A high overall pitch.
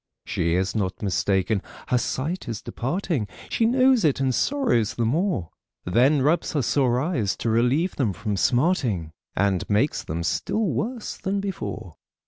No: low, 125 Hz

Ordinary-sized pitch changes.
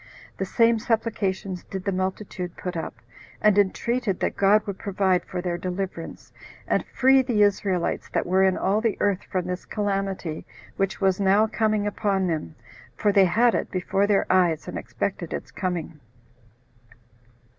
No: narrow, 2.3 semitones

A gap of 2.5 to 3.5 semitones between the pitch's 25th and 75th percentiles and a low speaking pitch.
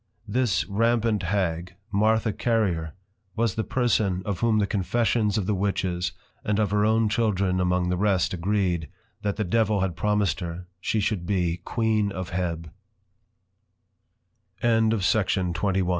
Yes: average, 3.1 semitones; low, 100 Hz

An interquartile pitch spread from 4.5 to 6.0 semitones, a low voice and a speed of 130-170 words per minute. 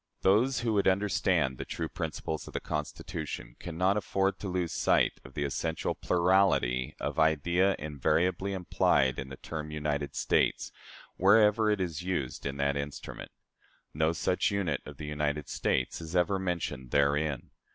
Yes: average, 4.8 semitones; very low, 80 Hz; average, 160 wpm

